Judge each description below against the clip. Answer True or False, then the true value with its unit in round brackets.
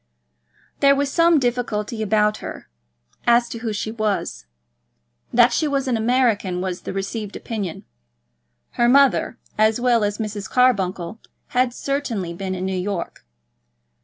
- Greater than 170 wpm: False (140 wpm)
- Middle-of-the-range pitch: False (220 Hz)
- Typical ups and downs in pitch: True (3.8 semitones)